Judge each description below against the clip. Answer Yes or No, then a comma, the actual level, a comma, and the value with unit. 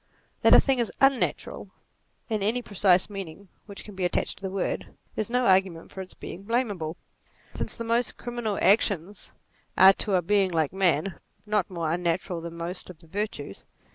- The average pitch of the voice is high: Yes, high, 195 Hz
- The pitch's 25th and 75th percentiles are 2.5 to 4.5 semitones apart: Yes, average, 3.5 semitones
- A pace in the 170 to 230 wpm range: Yes, average, 180 wpm